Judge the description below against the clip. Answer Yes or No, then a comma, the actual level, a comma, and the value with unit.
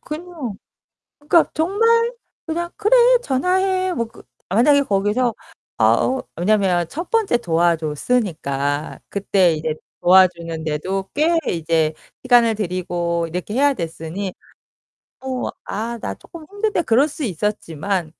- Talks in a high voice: Yes, high, 210 Hz